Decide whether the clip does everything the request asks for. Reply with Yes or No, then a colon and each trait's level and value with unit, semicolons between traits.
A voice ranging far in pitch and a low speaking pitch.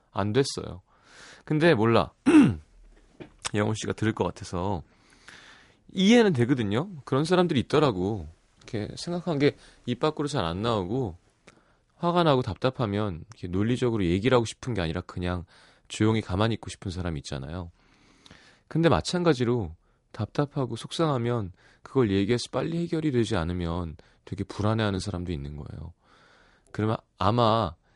Yes: wide, 6.1 semitones; low, 110 Hz